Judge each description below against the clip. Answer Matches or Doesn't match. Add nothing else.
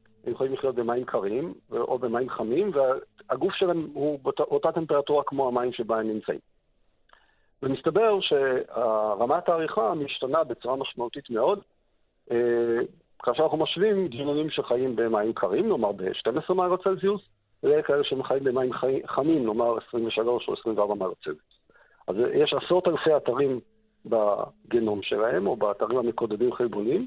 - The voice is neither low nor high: Matches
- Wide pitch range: Matches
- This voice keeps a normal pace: Matches